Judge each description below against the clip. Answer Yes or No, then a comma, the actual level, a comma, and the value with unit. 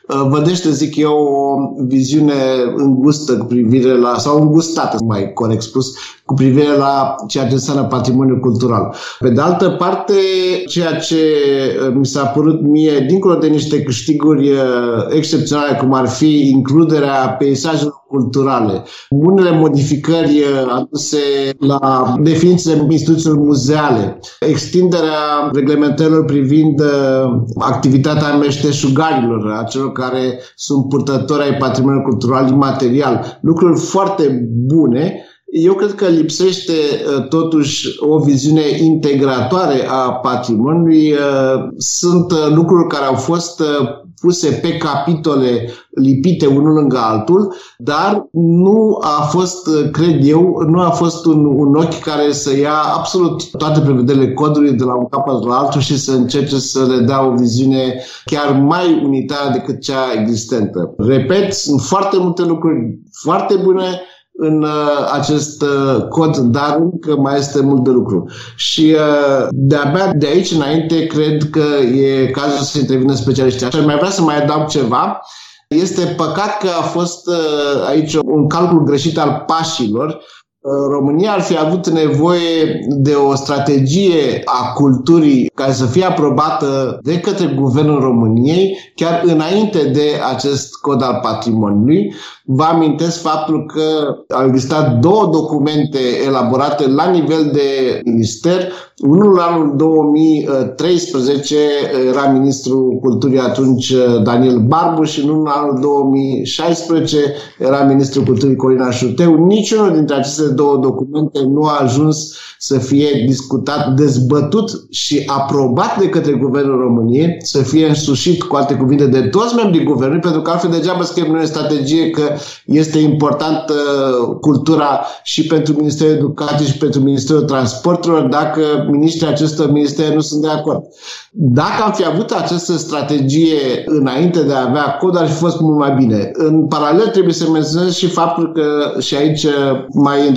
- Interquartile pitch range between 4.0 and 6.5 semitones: No, average, 3.0 semitones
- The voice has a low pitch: No, medium, 145 Hz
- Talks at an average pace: Yes, average, 140 wpm